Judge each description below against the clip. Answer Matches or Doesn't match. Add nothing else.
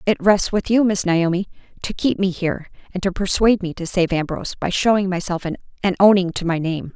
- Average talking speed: Doesn't match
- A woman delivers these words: Matches